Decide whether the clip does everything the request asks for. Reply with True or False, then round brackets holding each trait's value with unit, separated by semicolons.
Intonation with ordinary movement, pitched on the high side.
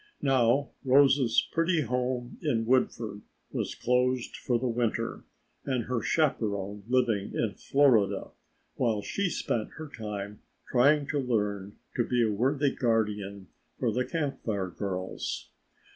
False (3.9 semitones; 120 Hz)